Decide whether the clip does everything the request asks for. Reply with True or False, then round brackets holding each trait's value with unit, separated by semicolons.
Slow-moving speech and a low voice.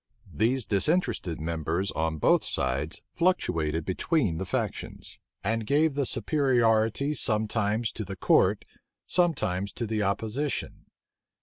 True (115 wpm; 110 Hz)